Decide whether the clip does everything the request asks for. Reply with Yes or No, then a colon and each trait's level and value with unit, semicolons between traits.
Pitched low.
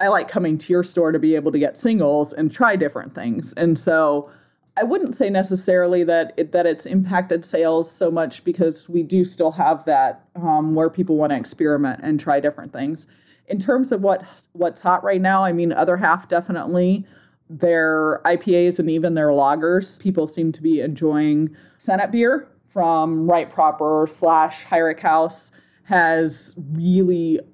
No: medium, 165 Hz